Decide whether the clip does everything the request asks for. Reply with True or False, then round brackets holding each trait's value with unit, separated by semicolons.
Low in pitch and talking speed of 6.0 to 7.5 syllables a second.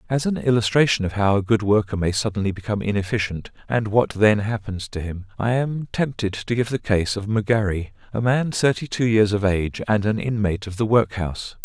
False (105 Hz; 5.5 syllables/s)